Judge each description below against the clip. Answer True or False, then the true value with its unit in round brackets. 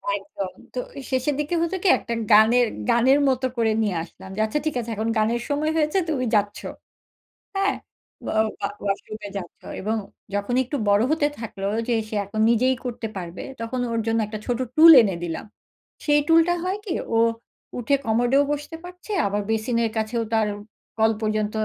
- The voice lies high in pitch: True (230 Hz)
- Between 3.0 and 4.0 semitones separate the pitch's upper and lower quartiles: False (5.0 semitones)